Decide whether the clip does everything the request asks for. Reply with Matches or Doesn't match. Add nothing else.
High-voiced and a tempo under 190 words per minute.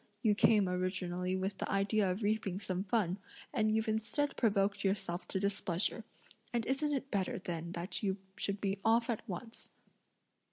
Matches